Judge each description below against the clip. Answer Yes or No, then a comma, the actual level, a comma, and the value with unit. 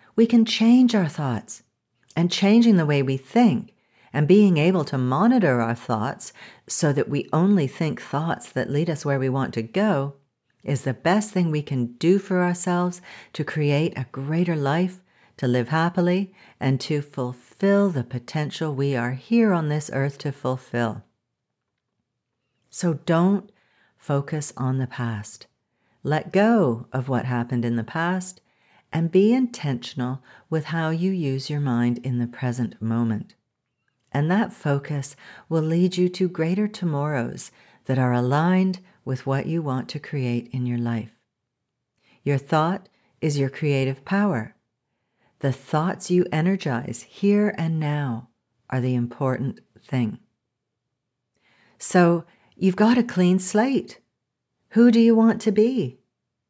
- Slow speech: No, average, 150 wpm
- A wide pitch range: Yes, wide, 6.3 semitones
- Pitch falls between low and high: Yes, medium, 150 Hz